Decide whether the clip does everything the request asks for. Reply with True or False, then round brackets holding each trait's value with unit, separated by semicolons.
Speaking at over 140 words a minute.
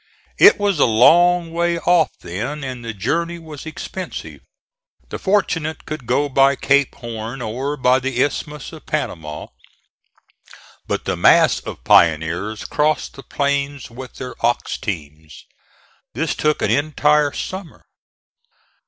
False (135 wpm)